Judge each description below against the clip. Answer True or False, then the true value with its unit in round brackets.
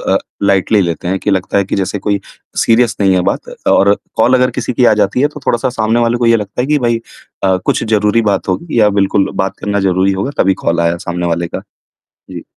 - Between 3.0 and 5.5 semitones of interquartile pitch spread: True (3.6 semitones)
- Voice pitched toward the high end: False (100 Hz)